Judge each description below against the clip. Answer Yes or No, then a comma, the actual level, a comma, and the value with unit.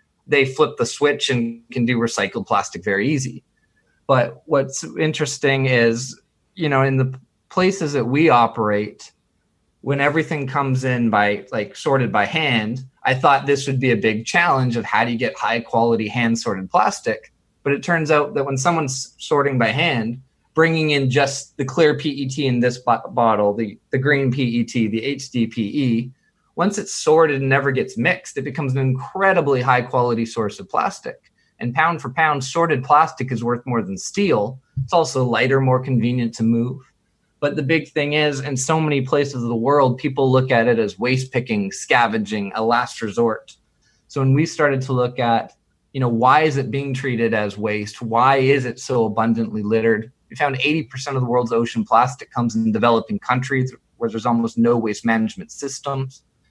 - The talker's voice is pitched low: Yes, low, 130 Hz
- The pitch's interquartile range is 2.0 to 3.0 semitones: No, average, 3.7 semitones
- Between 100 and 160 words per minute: No, average, 185 wpm